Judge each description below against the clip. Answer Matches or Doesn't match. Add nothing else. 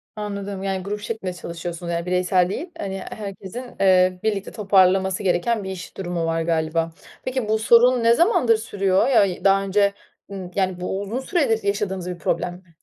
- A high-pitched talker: Matches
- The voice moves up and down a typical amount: Matches